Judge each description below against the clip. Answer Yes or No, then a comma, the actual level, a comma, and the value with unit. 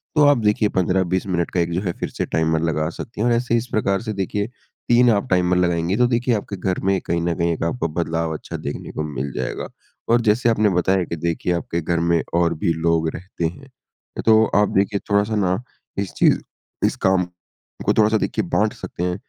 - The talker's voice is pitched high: No, very low, 95 Hz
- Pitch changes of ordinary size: Yes, average, 3.9 semitones